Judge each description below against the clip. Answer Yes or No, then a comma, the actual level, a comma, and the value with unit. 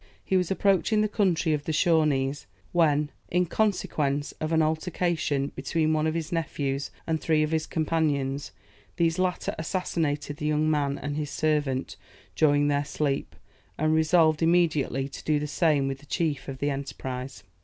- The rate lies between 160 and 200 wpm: Yes, average, 165 wpm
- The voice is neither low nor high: Yes, medium, 155 Hz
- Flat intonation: Yes, narrow, 2.3 semitones